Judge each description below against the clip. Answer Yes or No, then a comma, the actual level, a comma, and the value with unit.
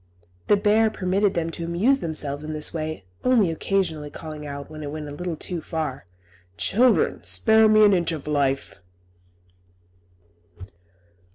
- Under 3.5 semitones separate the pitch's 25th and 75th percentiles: No, average, 5.0 semitones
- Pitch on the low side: No, medium, 165 Hz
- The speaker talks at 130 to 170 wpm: Yes, average, 150 wpm